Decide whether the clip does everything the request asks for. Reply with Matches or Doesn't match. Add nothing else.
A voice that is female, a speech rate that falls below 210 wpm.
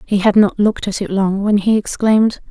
Doesn't match